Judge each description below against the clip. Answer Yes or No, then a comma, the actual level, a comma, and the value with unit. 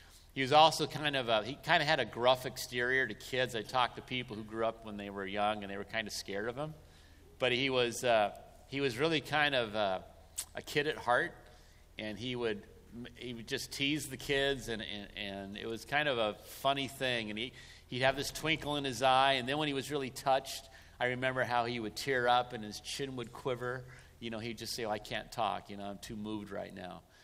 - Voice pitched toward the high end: No, low, 125 Hz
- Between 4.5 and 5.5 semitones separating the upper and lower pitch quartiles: No, average, 4.0 semitones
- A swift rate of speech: Yes, fast, 245 wpm